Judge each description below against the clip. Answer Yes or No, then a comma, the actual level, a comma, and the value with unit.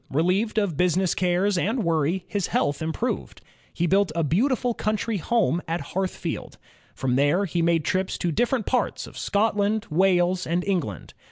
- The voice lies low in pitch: No, medium, 185 Hz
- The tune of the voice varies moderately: Yes, average, 3.6 semitones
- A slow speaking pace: No, average, 160 wpm